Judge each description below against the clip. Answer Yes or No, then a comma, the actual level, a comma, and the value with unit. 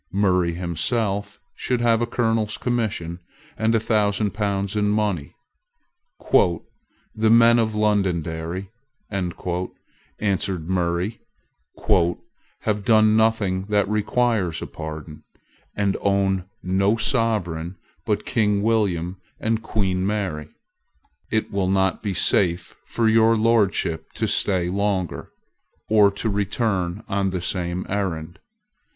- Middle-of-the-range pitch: No, low, 100 Hz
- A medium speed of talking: No, slow, 110 wpm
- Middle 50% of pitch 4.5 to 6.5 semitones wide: No, average, 3.2 semitones